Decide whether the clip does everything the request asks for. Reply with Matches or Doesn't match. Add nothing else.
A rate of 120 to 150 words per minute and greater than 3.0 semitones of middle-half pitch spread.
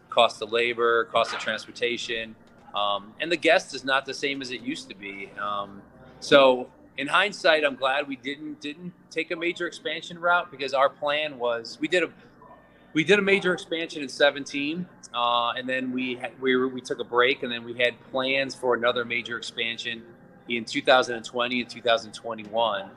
Doesn't match